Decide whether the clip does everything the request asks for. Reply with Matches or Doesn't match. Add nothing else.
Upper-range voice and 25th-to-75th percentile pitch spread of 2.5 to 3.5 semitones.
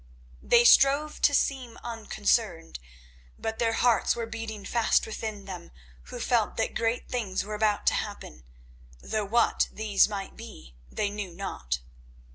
Matches